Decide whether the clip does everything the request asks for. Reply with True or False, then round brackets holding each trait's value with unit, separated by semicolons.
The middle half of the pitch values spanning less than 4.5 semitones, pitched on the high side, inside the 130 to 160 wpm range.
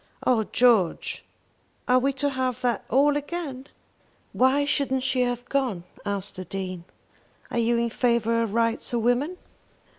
True (2.7 semitones; 245 Hz; 150 wpm)